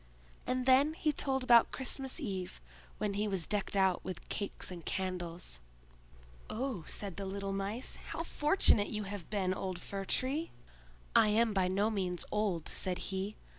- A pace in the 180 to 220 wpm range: No, average, 165 wpm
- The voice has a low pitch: No, high, 200 Hz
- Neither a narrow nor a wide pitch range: Yes, average, 4.6 semitones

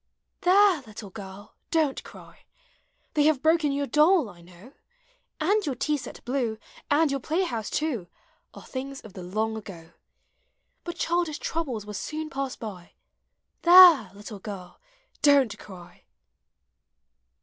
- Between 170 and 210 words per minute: No, average, 140 wpm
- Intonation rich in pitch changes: Yes, wide, 7.1 semitones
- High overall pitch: Yes, very high, 270 Hz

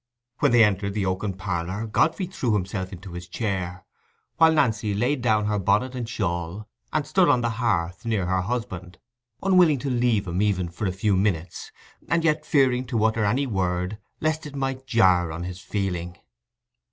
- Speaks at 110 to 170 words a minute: No, average, 180 wpm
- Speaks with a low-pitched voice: Yes, low, 105 Hz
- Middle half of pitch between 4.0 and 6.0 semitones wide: Yes, average, 5.0 semitones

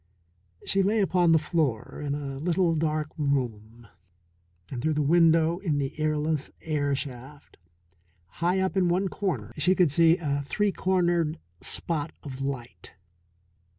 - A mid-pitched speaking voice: Yes, medium, 155 Hz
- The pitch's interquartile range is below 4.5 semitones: Yes, average, 3.8 semitones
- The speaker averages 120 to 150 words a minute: Yes, average, 145 wpm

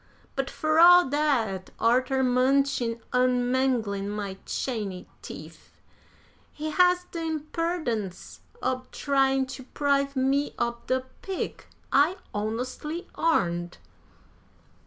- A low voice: No, very high, 265 Hz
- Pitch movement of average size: Yes, average, 4.4 semitones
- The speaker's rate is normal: No, slow, 105 wpm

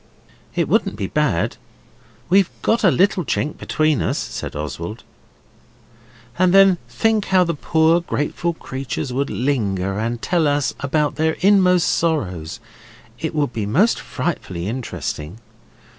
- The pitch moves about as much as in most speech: No, wide, 7.5 semitones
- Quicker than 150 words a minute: No, slow, 135 wpm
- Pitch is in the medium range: Yes, medium, 150 Hz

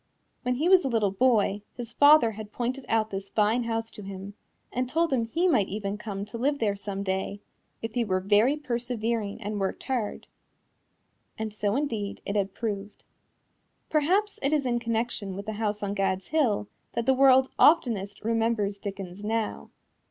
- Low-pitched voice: No, high, 225 Hz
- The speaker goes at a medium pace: Yes, average, 180 wpm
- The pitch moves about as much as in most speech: Yes, average, 3.8 semitones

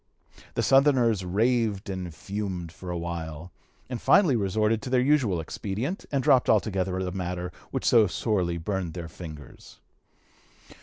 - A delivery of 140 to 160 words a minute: Yes, average, 145 wpm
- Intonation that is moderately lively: Yes, average, 4.8 semitones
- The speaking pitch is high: No, very low, 95 Hz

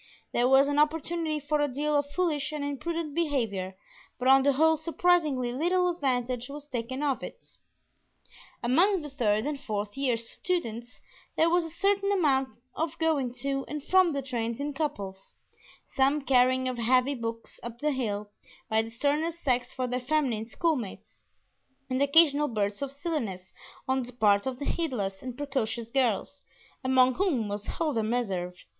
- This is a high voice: Yes, very high, 270 Hz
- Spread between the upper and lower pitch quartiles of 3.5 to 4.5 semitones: Yes, average, 4.2 semitones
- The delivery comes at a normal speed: Yes, average, 165 wpm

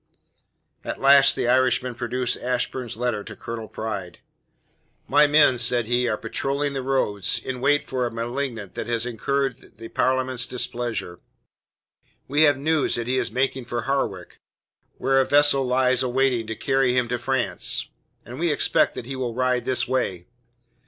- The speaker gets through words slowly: No, average, 165 wpm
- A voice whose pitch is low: Yes, low, 125 Hz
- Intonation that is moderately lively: No, narrow, 2.2 semitones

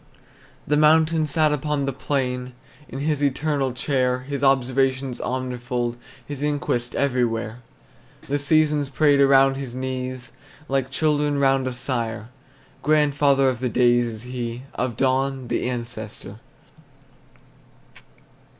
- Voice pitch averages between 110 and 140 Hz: Yes, low, 135 Hz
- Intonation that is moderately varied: No, narrow, 2.3 semitones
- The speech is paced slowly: Yes, slow, 120 wpm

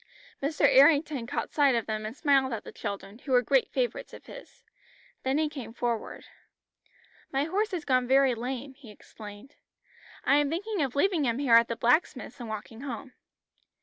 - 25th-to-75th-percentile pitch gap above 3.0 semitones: Yes, average, 3.8 semitones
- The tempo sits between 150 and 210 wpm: Yes, average, 180 wpm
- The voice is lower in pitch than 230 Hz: No, very high, 265 Hz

